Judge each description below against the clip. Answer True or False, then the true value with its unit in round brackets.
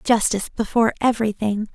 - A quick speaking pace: False (105 wpm)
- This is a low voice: False (220 Hz)